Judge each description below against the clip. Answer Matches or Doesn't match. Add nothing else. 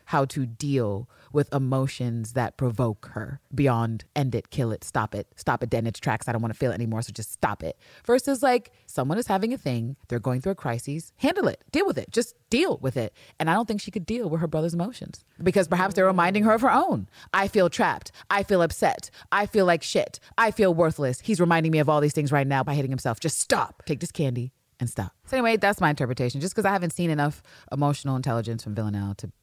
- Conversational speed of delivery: Doesn't match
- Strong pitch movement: Matches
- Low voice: Doesn't match